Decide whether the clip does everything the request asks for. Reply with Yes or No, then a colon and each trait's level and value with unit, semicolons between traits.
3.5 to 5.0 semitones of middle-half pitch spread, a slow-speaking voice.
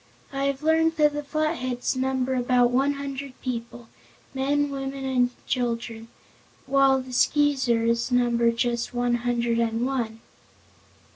No: narrow, 2.5 semitones; slow, 130 wpm